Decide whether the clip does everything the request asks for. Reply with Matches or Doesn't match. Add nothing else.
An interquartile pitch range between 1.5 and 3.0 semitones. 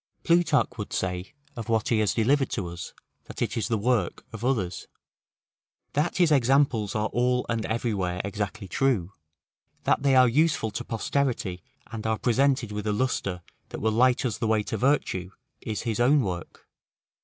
Doesn't match